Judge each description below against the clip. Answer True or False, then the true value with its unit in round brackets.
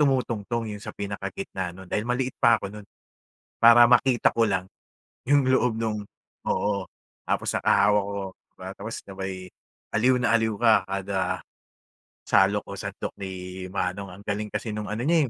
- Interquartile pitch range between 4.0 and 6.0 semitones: False (3.3 semitones)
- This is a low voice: True (105 Hz)